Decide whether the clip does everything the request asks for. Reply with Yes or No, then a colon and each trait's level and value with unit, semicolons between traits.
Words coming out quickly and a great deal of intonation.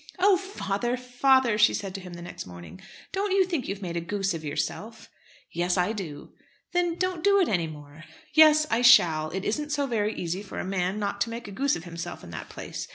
Yes: fast, 225 wpm; wide, 8.2 semitones